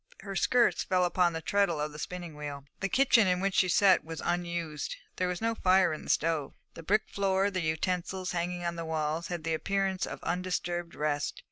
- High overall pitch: No, medium, 175 Hz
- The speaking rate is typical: No, fast, 210 wpm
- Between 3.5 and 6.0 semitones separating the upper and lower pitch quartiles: No, average, 2.8 semitones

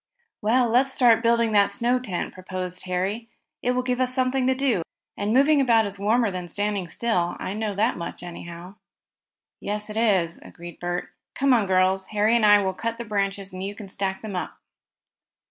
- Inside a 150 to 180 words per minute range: No, average, 195 wpm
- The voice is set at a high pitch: Yes, high, 210 Hz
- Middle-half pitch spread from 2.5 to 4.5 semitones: Yes, average, 4.0 semitones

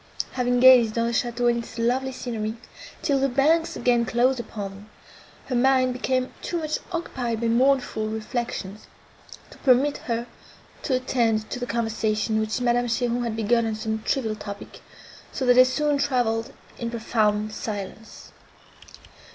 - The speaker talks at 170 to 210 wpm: No, average, 155 wpm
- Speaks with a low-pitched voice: No, high, 240 Hz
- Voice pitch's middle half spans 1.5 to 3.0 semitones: Yes, narrow, 2.6 semitones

